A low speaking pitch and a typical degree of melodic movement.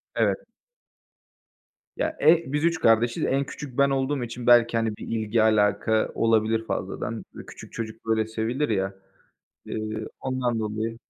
Yes: low, 115 Hz; average, 3.1 semitones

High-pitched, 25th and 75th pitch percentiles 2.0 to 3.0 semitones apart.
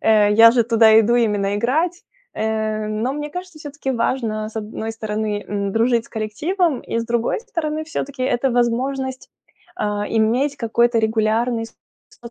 No: high, 230 Hz; average, 3.5 semitones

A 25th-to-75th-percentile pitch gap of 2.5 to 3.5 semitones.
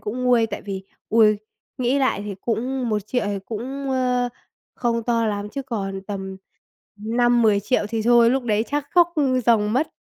Yes: average, 3.2 semitones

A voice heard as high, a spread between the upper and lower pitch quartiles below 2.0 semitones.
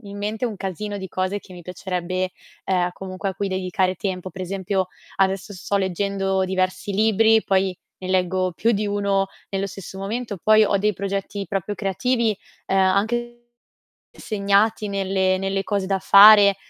Yes: high, 195 Hz; narrow, 1.5 semitones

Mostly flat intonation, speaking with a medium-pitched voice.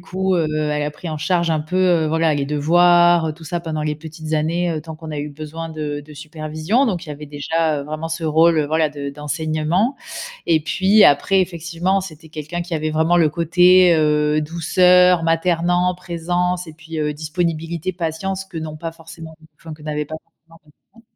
Yes: narrow, 2.3 semitones; medium, 160 Hz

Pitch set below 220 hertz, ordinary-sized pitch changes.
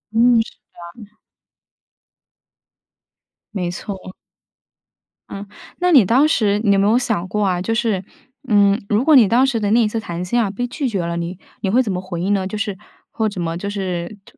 Yes: high, 205 Hz; average, 3.5 semitones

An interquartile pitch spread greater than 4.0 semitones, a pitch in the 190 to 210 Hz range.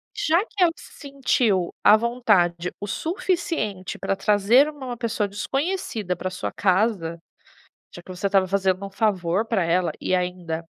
Yes: average, 5.3 semitones; high, 200 Hz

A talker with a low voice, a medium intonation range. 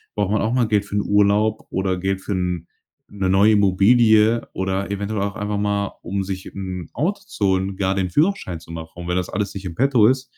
No: low, 100 Hz; narrow, 2.2 semitones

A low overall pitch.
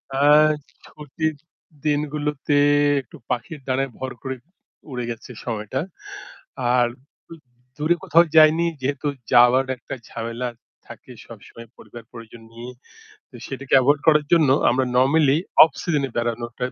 Yes: low, 130 Hz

